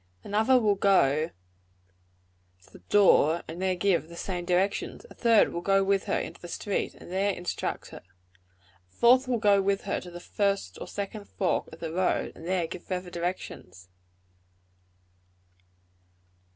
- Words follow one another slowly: No, average, 165 wpm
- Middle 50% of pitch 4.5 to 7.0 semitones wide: No, average, 2.9 semitones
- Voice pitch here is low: No, medium, 185 Hz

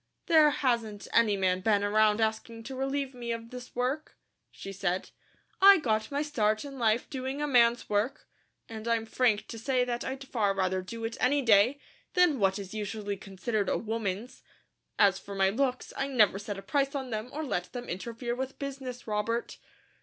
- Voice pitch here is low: No, high, 230 Hz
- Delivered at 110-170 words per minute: No, average, 190 wpm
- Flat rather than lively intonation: No, average, 4.1 semitones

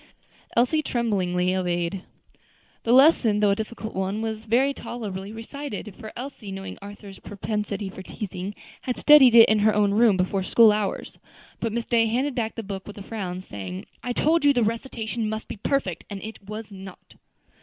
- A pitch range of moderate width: Yes, average, 3.3 semitones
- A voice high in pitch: Yes, high, 215 Hz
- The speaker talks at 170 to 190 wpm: Yes, average, 180 wpm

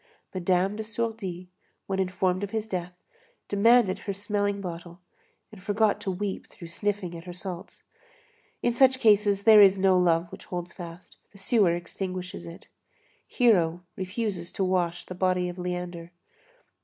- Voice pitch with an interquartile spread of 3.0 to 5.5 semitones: No, narrow, 2.6 semitones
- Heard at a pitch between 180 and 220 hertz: Yes, medium, 185 Hz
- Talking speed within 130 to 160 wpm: Yes, average, 155 wpm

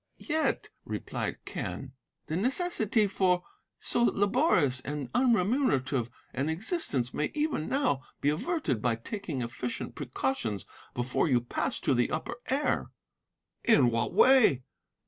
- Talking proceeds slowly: Yes, slow, 125 wpm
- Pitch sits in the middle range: Yes, medium, 155 Hz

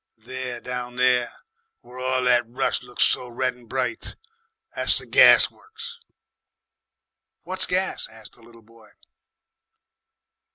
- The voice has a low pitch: Yes, low, 125 Hz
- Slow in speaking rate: Yes, slow, 125 wpm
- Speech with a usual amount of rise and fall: No, narrow, 1.4 semitones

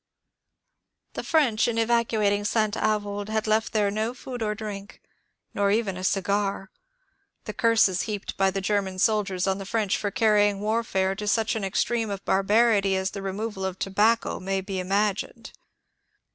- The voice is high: Yes, high, 205 Hz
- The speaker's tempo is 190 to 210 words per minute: No, average, 170 wpm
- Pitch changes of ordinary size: No, narrow, 2.1 semitones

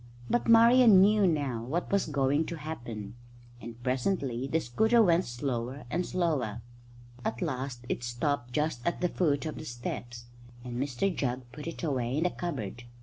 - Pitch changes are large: Yes, wide, 6.1 semitones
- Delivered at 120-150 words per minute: No, average, 170 wpm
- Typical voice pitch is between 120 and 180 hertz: Yes, medium, 140 Hz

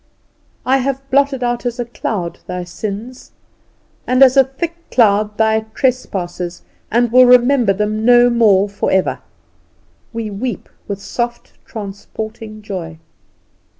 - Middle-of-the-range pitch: No, high, 225 Hz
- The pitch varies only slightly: No, average, 3.7 semitones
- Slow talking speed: Yes, slow, 130 wpm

